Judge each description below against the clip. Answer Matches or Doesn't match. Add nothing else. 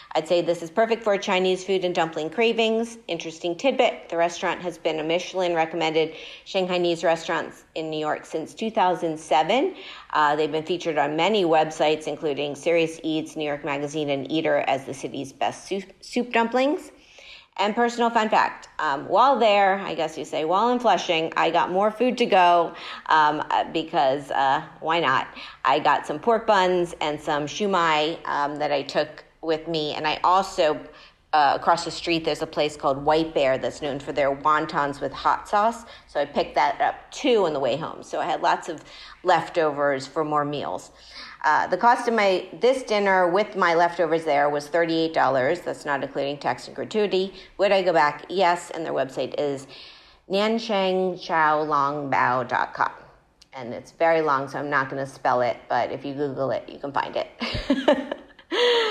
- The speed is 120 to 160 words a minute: Doesn't match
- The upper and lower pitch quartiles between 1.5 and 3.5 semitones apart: Doesn't match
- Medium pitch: Matches